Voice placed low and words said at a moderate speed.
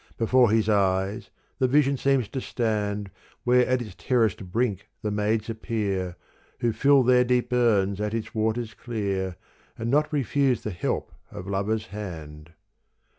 Yes: low, 110 Hz; average, 150 wpm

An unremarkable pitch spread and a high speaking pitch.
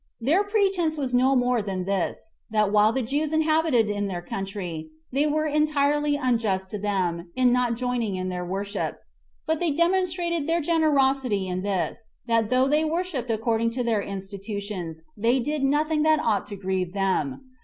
No: wide, 7.2 semitones; high, 245 Hz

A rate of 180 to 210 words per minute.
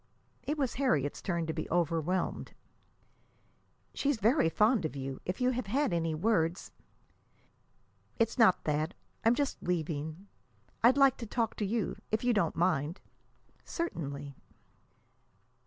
No: average, 140 wpm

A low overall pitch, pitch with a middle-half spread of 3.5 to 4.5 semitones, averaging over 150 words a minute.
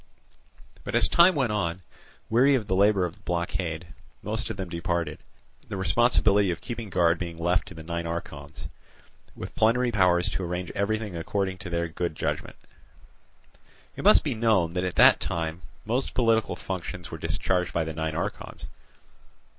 Yes: very low, 90 Hz; average, 4.1 semitones; average, 165 wpm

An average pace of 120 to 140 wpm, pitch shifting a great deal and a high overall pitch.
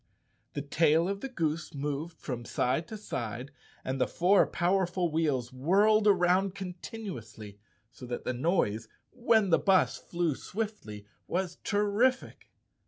No: slow, 135 wpm; wide, 6.9 semitones; medium, 170 Hz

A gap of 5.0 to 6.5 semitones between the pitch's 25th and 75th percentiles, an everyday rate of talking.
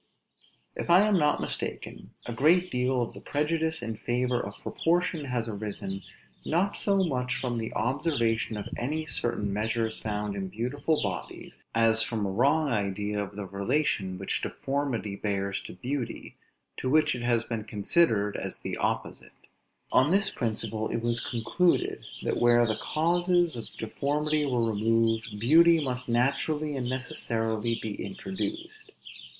Yes: wide, 5.6 semitones; average, 150 wpm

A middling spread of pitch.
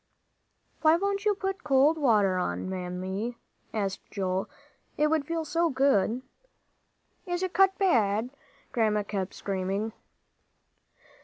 No: wide, 8.8 semitones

